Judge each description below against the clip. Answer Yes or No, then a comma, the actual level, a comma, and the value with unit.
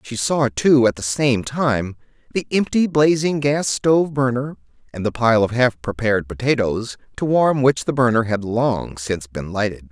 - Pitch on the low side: Yes, low, 120 Hz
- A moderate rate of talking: Yes, average, 180 wpm